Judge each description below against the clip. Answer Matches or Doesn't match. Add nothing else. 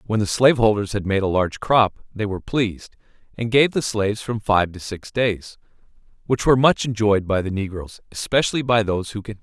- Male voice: Matches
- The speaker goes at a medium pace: Doesn't match